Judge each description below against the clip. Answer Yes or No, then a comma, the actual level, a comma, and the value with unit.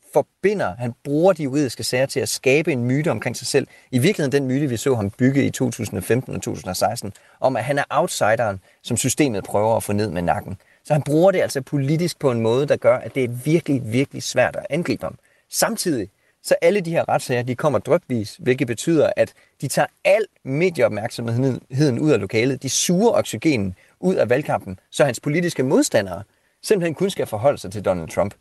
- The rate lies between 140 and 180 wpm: No, average, 205 wpm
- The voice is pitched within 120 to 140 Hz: Yes, low, 135 Hz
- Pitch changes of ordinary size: Yes, average, 4.2 semitones